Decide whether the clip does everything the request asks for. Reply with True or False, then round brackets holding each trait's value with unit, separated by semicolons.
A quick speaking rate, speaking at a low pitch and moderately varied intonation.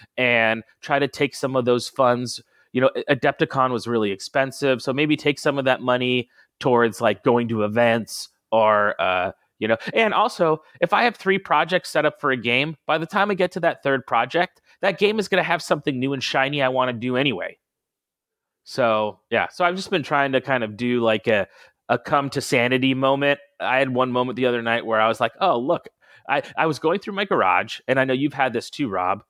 True (230 wpm; 130 Hz; 3.7 semitones)